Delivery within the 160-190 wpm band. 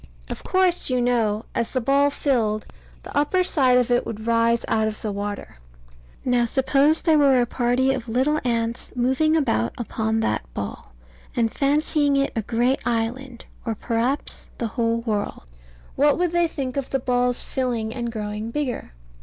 Yes: average, 170 wpm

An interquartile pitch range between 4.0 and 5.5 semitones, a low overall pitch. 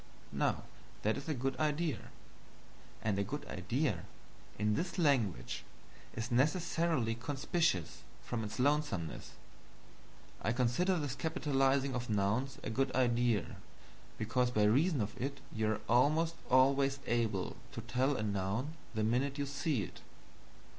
Yes: average, 4.6 semitones; low, 125 Hz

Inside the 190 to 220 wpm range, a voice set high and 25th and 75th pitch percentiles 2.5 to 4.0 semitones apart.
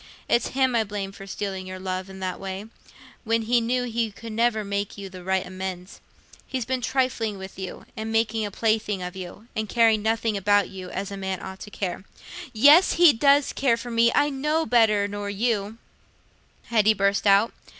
Yes: average, 195 wpm; high, 215 Hz; average, 3.1 semitones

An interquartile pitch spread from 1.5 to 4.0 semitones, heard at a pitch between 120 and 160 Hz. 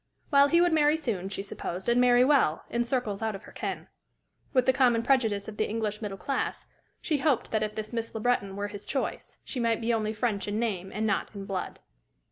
No: average, 3.6 semitones; high, 225 Hz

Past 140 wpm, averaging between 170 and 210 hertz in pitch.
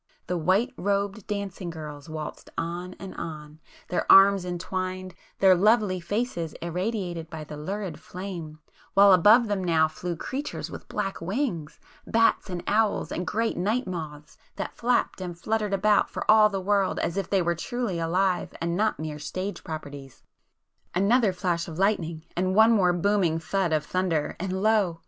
Yes: average, 160 wpm; medium, 185 Hz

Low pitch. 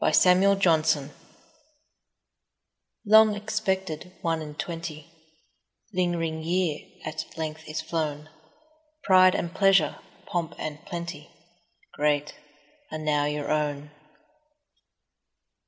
No: medium, 160 Hz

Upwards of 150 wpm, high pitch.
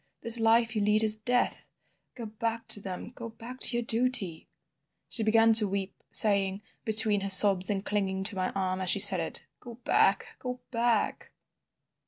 Yes: average, 175 wpm; high, 215 Hz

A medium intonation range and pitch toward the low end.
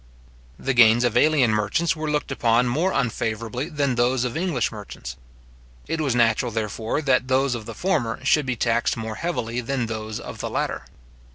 Yes: average, 3.5 semitones; low, 120 Hz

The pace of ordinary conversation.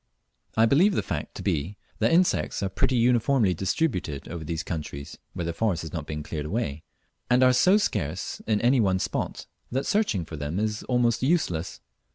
Yes: average, 190 wpm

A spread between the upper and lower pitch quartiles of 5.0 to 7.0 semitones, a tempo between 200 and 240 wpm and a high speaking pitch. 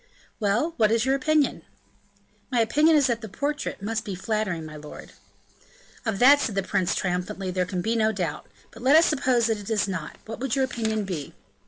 Yes: average, 5.3 semitones; fast, 205 wpm; high, 220 Hz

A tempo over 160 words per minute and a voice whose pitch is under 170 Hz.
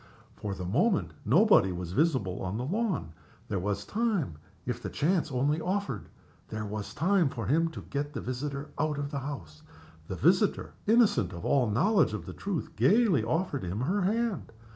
Yes: average, 180 wpm; medium, 140 Hz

